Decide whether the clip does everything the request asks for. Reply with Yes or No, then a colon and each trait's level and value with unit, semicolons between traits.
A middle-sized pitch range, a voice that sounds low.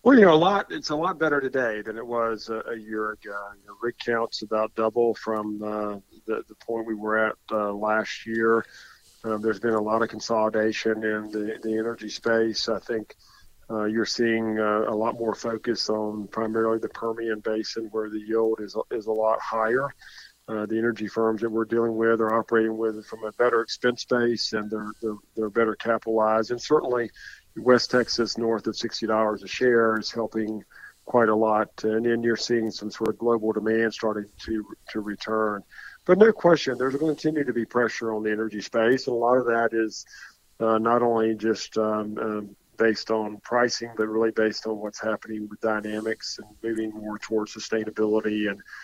No: narrow, 1.2 semitones; low, 110 Hz